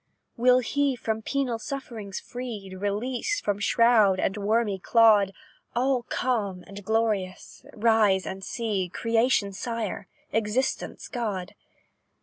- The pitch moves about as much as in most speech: Yes, average, 3.3 semitones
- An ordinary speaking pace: No, slow, 115 wpm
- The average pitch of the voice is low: No, high, 220 Hz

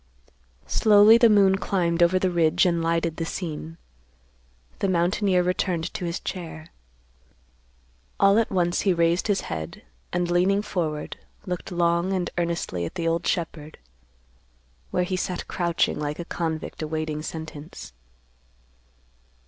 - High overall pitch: No, medium, 175 Hz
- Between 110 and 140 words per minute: Yes, slow, 135 wpm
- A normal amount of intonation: No, narrow, 2.1 semitones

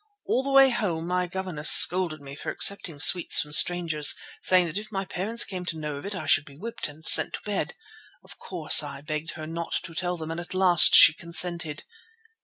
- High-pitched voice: No, medium, 170 Hz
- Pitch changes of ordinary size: Yes, average, 3.3 semitones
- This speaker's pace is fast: Yes, fast, 215 wpm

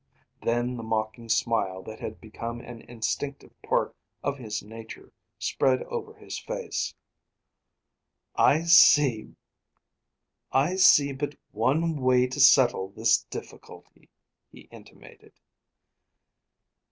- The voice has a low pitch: Yes, low, 125 Hz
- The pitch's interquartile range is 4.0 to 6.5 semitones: Yes, average, 4.3 semitones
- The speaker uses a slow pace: Yes, slow, 100 wpm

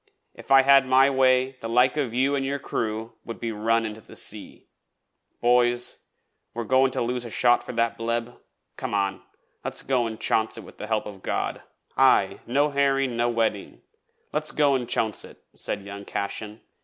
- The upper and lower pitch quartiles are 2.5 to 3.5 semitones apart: Yes, average, 2.9 semitones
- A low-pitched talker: Yes, low, 120 Hz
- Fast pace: No, average, 190 wpm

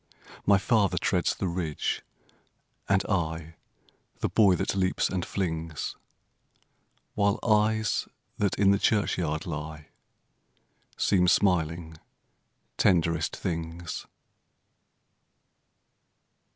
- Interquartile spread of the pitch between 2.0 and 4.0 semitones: Yes, average, 3.6 semitones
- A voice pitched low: Yes, very low, 90 Hz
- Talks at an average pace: No, slow, 85 wpm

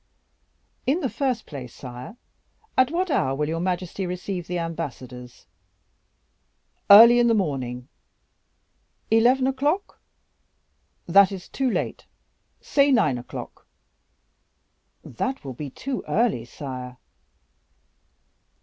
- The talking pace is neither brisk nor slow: No, slow, 105 wpm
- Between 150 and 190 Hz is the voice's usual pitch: Yes, medium, 185 Hz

